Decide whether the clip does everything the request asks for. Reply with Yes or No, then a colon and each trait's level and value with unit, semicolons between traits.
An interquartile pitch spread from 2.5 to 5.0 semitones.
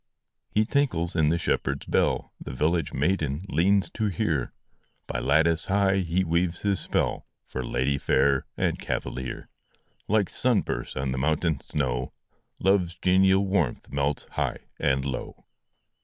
No: wide, 5.6 semitones